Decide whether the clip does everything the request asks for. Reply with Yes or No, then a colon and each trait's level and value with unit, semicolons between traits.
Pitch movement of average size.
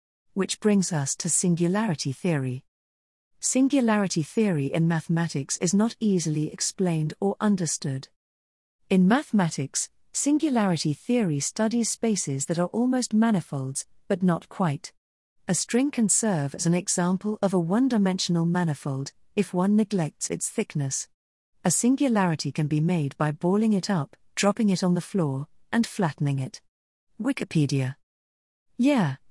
No: wide, 6.3 semitones